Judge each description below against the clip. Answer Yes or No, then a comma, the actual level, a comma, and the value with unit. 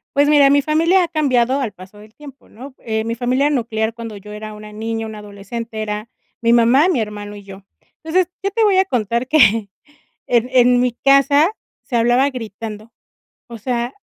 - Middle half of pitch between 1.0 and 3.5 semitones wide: No, average, 4.2 semitones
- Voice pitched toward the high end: Yes, high, 235 Hz